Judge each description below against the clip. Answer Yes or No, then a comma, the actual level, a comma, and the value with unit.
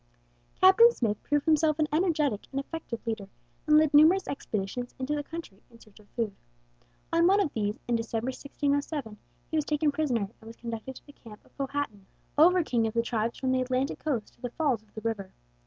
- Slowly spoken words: No, fast, 205 wpm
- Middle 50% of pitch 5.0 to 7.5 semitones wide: Yes, average, 5.3 semitones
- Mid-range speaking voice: No, very high, 260 Hz